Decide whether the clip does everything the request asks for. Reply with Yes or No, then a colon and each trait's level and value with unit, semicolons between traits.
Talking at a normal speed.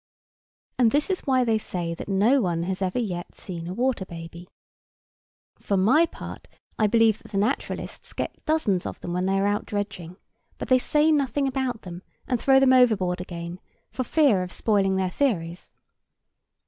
Yes: average, 180 wpm